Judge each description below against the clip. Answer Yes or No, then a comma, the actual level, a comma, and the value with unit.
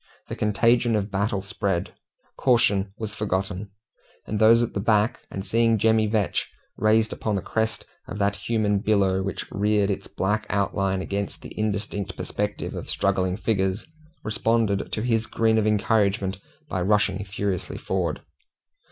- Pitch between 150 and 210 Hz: No, low, 105 Hz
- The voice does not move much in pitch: Yes, narrow, 2.1 semitones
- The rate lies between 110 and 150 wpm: Yes, average, 145 wpm